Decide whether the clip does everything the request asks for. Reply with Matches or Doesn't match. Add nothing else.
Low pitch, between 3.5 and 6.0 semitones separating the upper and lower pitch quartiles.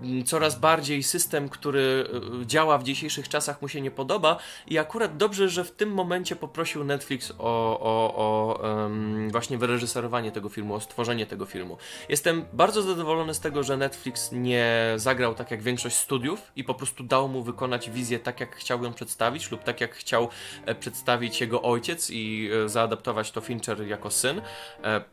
Matches